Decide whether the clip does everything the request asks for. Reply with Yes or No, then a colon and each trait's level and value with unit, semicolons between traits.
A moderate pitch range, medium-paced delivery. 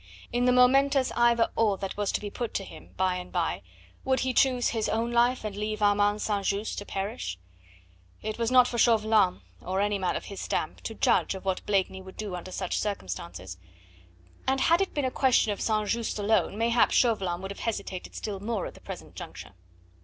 No: average, 3.6 semitones; fast, 210 wpm